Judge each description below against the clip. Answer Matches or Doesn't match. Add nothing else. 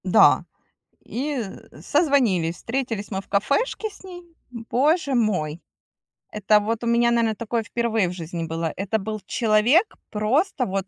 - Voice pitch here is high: Matches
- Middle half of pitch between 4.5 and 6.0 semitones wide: Matches